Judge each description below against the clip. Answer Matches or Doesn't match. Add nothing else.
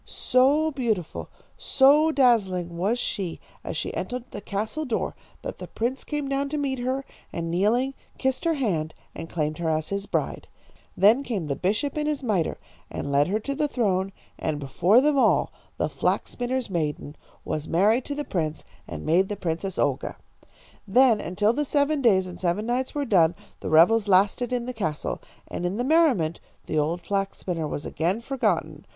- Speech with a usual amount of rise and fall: Doesn't match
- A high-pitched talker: Matches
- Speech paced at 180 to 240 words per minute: Matches